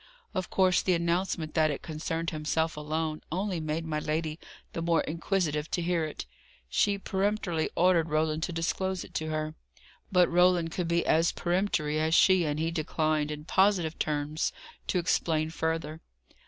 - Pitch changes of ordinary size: No, narrow, 2.3 semitones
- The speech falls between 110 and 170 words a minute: Yes, average, 165 wpm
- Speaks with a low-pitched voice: No, medium, 165 Hz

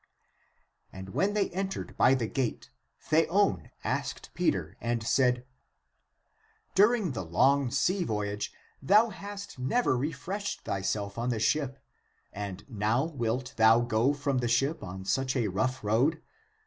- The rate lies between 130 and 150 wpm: Yes, average, 145 wpm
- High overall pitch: No, low, 130 Hz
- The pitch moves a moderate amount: No, wide, 6.8 semitones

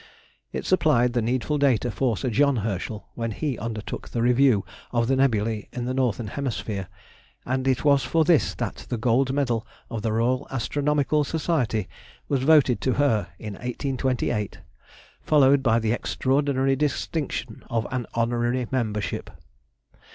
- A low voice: Yes, low, 125 Hz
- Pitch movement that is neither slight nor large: Yes, average, 3.2 semitones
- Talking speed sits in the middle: Yes, average, 150 wpm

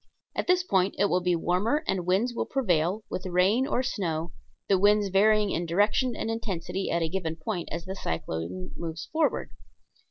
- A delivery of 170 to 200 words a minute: Yes, average, 185 wpm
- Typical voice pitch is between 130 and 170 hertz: No, high, 190 Hz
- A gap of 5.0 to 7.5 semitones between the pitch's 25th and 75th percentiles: No, average, 4.0 semitones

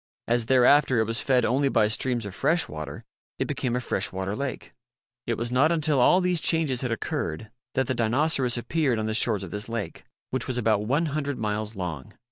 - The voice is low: Yes, low, 120 Hz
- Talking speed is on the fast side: Yes, fast, 210 wpm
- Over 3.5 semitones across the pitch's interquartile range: Yes, average, 4.3 semitones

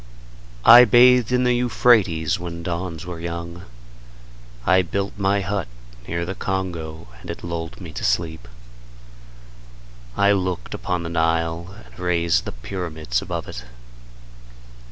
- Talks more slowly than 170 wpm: Yes, slow, 135 wpm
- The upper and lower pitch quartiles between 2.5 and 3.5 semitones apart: Yes, average, 2.9 semitones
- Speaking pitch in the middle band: No, very low, 85 Hz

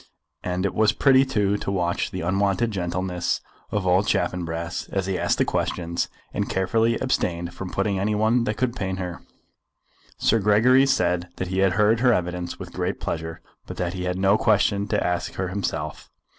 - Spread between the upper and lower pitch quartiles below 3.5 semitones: Yes, average, 3.0 semitones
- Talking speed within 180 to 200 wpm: Yes, average, 185 wpm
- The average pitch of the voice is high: No, very low, 95 Hz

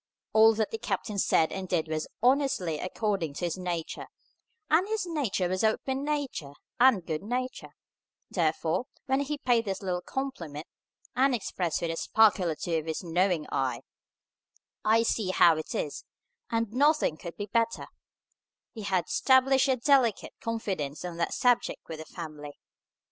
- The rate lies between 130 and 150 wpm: No, average, 160 wpm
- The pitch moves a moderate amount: No, wide, 7.1 semitones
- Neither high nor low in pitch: No, high, 200 Hz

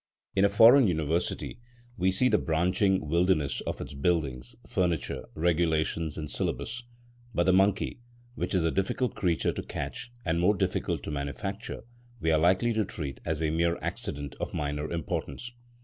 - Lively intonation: No, average, 3.9 semitones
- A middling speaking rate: Yes, average, 165 wpm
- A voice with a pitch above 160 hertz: No, very low, 85 Hz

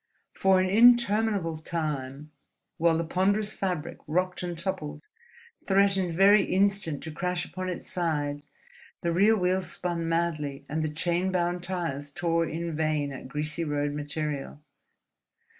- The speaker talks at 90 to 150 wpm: Yes, average, 140 wpm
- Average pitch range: Yes, average, 3.5 semitones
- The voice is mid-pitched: Yes, medium, 170 Hz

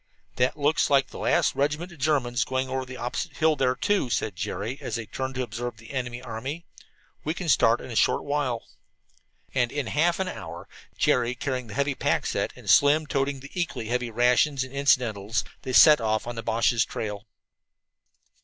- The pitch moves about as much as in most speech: Yes, average, 3.4 semitones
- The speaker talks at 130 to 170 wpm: No, average, 195 wpm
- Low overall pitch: Yes, low, 130 Hz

